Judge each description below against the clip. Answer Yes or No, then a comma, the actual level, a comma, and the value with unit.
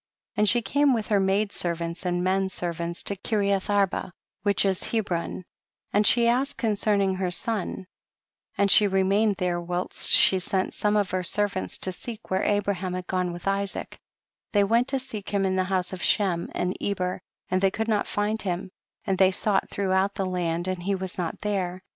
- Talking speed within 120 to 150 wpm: No, average, 195 wpm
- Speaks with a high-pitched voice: Yes, high, 195 Hz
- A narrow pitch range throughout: Yes, narrow, 2.1 semitones